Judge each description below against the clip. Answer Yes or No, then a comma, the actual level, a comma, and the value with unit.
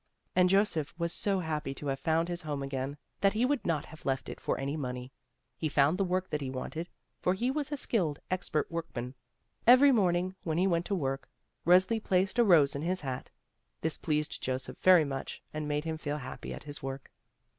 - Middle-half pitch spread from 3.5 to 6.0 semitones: Yes, average, 4.7 semitones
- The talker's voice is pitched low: No, medium, 160 Hz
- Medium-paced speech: No, fast, 210 wpm